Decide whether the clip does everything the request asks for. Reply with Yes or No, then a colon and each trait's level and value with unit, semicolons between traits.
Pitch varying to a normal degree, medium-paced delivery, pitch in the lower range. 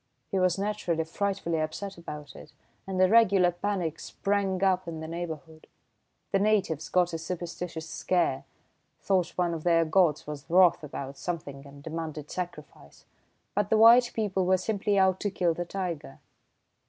No: average, 3.2 semitones; average, 160 wpm; medium, 175 Hz